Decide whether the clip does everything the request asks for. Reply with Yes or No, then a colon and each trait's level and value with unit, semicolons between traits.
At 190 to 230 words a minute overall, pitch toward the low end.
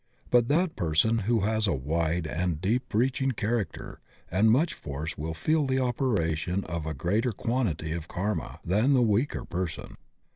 No: average, 170 wpm; low, 100 Hz